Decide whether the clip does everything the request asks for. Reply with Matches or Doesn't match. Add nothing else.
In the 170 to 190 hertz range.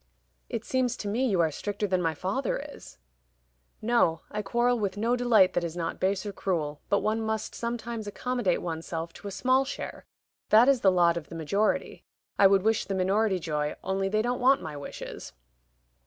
Doesn't match